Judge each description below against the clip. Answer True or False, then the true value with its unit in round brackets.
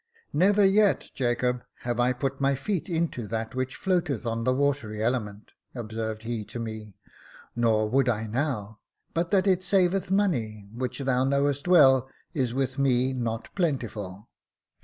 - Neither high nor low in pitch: False (130 Hz)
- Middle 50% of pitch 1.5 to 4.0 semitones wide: False (4.5 semitones)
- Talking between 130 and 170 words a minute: True (160 wpm)